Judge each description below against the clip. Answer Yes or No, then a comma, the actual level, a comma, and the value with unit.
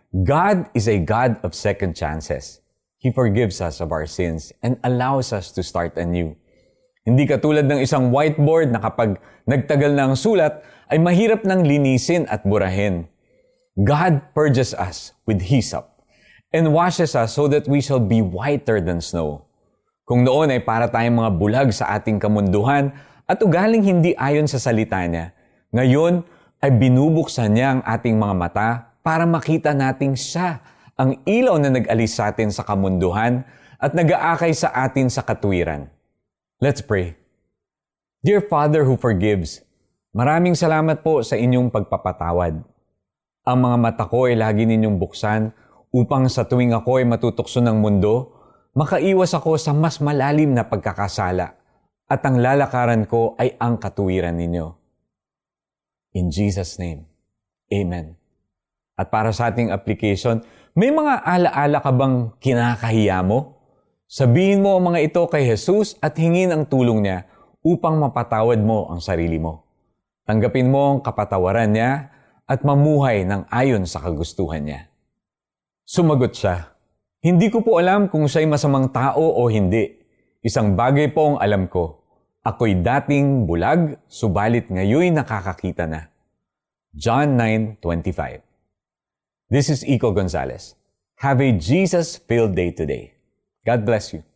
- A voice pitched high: No, low, 120 Hz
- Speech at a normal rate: Yes, average, 145 wpm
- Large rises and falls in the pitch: Yes, wide, 6.0 semitones